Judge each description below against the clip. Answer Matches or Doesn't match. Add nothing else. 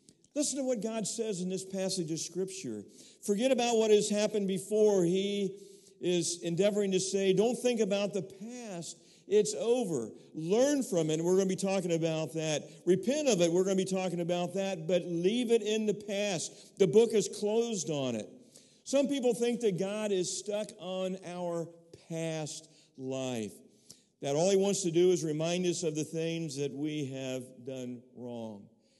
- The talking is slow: Doesn't match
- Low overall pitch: Doesn't match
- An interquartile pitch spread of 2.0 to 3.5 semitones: Doesn't match